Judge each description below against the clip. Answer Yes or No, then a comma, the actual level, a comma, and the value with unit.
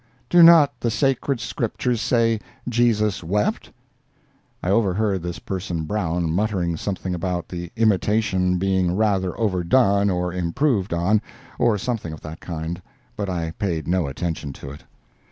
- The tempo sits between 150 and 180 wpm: No, average, 140 wpm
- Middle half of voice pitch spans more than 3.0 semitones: Yes, average, 4.0 semitones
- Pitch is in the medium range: No, very low, 95 Hz